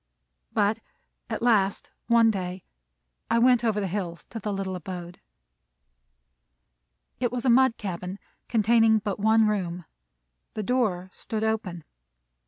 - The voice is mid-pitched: No, high, 210 Hz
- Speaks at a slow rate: Yes, slow, 130 wpm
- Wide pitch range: No, average, 3.7 semitones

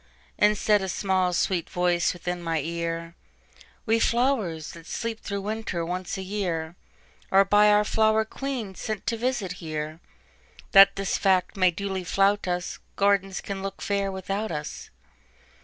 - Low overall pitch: No, high, 195 Hz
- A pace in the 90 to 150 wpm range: Yes, average, 140 wpm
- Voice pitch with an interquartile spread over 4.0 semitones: No, average, 3.0 semitones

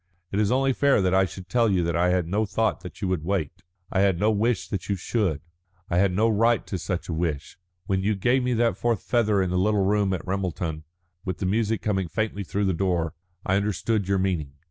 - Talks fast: Yes, fast, 235 wpm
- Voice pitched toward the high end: No, very low, 95 Hz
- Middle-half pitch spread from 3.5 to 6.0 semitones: No, average, 3.0 semitones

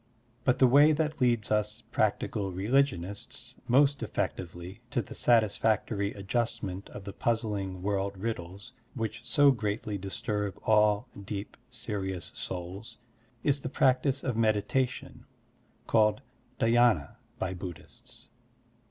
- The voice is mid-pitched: No, low, 110 Hz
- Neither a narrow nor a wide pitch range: Yes, average, 3.7 semitones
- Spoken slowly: Yes, slow, 115 wpm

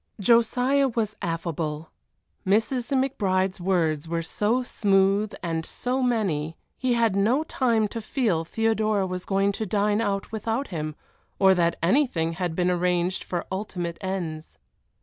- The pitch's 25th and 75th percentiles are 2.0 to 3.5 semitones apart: No, average, 4.7 semitones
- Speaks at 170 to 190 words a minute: No, average, 140 wpm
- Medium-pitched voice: No, high, 195 Hz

